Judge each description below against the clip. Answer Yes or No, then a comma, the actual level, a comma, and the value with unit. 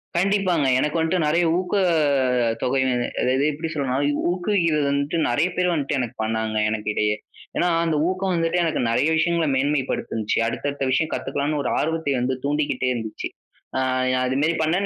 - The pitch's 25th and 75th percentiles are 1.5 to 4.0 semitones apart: No, average, 4.4 semitones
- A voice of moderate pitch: Yes, medium, 150 Hz